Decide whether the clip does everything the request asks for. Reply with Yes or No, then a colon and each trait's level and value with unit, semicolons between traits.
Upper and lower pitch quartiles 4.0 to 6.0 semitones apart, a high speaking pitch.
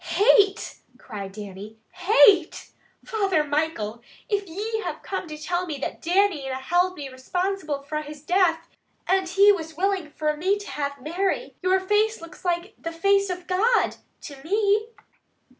Yes: average, 4.7 semitones; very high, 350 Hz